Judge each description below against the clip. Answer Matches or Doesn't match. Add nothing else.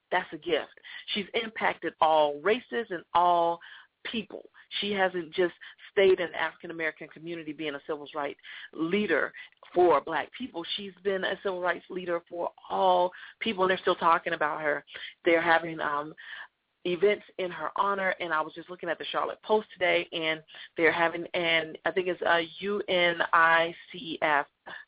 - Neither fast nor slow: Matches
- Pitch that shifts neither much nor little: Matches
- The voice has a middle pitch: Matches